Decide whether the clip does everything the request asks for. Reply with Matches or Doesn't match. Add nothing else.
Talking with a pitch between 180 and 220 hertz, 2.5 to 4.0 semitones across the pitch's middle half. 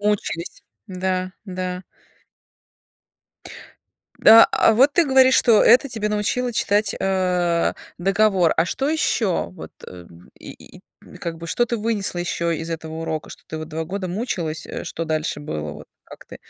Doesn't match